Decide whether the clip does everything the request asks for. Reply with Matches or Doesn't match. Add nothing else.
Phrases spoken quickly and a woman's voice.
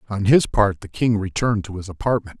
Doesn't match